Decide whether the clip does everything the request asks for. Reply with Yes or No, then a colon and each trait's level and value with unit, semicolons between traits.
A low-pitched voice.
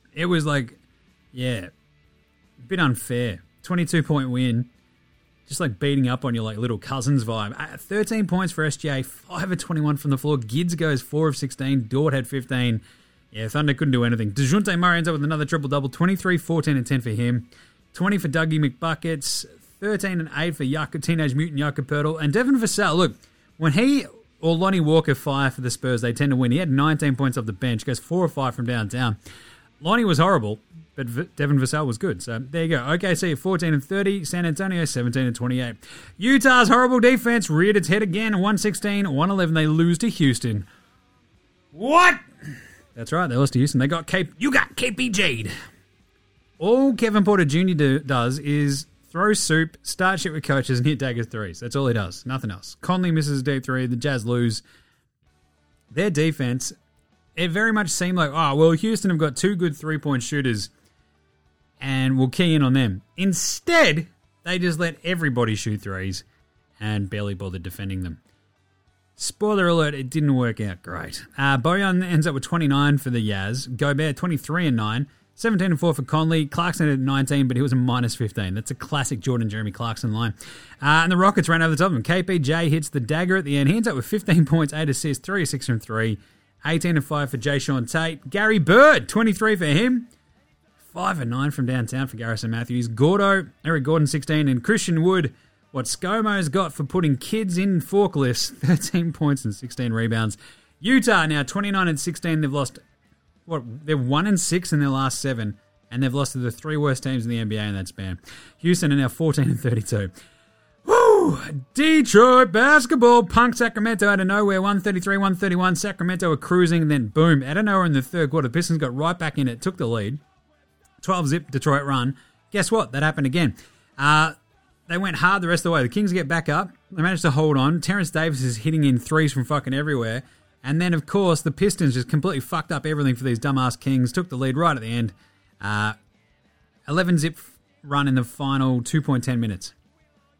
No: medium, 145 Hz